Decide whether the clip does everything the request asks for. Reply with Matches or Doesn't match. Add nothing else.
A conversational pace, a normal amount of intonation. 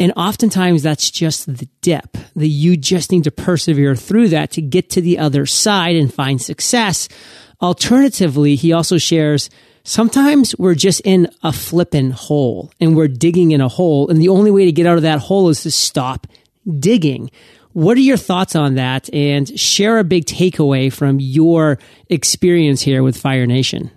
Matches